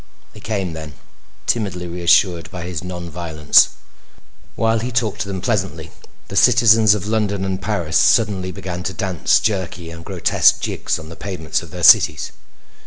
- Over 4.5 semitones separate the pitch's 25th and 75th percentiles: No, average, 3.4 semitones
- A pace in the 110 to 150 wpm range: No, average, 165 wpm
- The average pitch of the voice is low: Yes, very low, 95 Hz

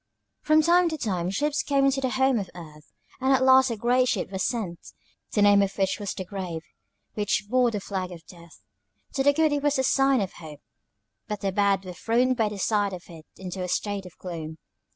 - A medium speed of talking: No, fast, 225 wpm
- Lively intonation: Yes, wide, 6.2 semitones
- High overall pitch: Yes, high, 205 Hz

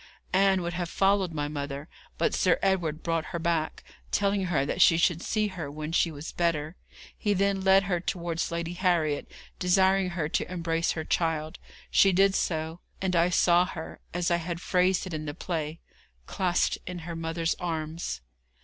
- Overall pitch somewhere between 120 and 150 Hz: No, medium, 170 Hz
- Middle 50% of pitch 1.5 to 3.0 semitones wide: Yes, narrow, 2.4 semitones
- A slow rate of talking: No, average, 180 wpm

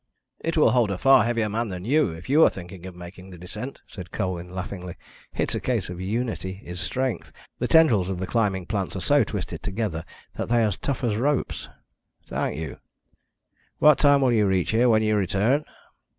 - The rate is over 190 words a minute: Yes, fast, 205 wpm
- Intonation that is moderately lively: Yes, average, 4.8 semitones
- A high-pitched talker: No, low, 105 Hz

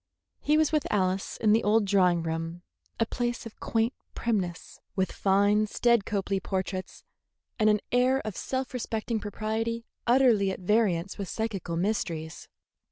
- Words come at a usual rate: Yes, average, 150 wpm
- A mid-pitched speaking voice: No, high, 210 Hz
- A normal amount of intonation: Yes, average, 3.4 semitones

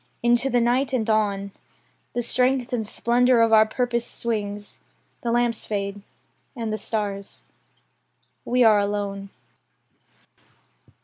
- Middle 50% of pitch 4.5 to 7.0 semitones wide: No, average, 2.8 semitones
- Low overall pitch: No, high, 225 Hz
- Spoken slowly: Yes, slow, 120 wpm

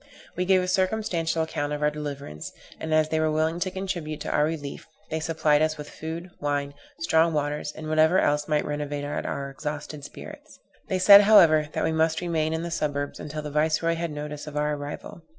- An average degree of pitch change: No, narrow, 1.9 semitones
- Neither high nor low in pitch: Yes, medium, 155 Hz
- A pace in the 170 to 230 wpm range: Yes, fast, 205 wpm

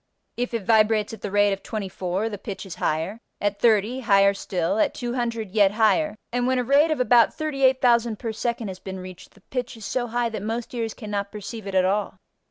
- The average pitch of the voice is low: No, high, 220 Hz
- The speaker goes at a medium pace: No, fast, 215 wpm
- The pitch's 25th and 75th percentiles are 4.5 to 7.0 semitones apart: No, average, 3.3 semitones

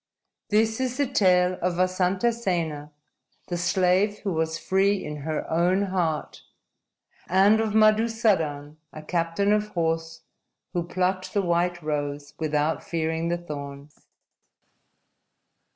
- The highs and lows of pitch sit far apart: No, average, 3.8 semitones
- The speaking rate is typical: No, slow, 120 wpm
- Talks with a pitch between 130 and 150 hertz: No, medium, 175 Hz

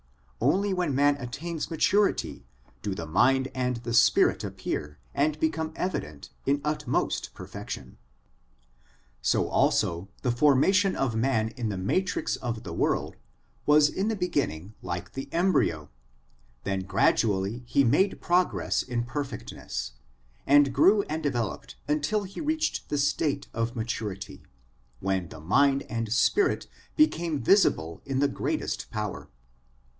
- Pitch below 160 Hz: Yes, low, 135 Hz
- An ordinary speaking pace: No, slow, 130 wpm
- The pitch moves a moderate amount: No, wide, 6.8 semitones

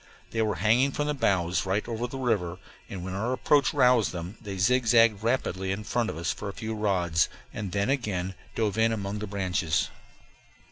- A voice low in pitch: Yes, low, 105 Hz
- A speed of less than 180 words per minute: No, average, 195 wpm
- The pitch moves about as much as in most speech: Yes, average, 3.7 semitones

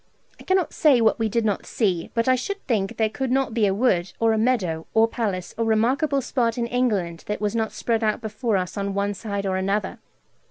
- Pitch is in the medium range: No, high, 220 Hz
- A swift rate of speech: Yes, fast, 230 wpm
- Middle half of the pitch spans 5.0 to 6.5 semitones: No, average, 3.3 semitones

